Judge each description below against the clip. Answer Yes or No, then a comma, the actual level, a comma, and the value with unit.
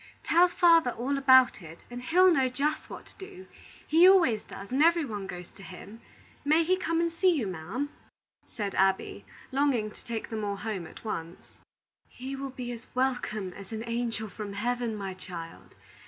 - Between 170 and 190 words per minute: Yes, average, 185 wpm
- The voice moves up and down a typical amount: No, wide, 6.6 semitones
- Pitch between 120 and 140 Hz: No, high, 245 Hz